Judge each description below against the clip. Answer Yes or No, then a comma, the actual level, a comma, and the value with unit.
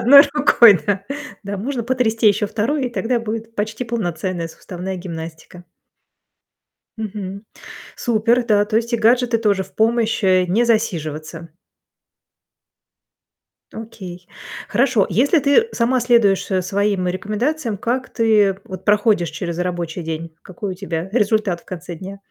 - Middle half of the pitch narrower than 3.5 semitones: No, average, 4.1 semitones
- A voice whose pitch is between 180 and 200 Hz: No, high, 210 Hz